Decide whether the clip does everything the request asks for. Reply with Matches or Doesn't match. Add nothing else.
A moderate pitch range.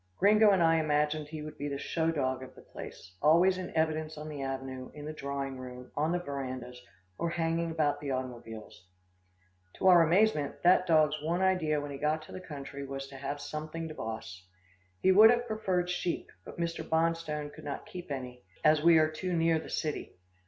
Matches